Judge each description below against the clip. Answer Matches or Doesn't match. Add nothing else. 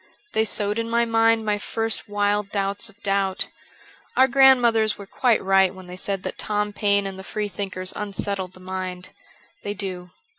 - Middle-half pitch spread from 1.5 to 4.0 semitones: Matches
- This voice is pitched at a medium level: Doesn't match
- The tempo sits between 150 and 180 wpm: Matches